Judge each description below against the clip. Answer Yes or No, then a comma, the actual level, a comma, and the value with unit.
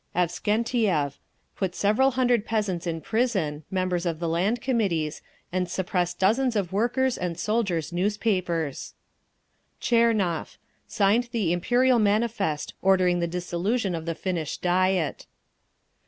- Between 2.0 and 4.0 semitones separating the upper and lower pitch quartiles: No, average, 4.6 semitones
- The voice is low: No, high, 190 Hz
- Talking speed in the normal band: No, slow, 120 wpm